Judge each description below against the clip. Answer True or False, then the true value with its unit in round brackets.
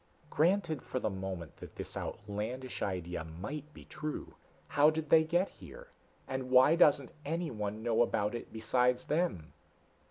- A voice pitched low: True (130 Hz)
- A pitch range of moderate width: False (6.8 semitones)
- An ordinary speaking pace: True (150 wpm)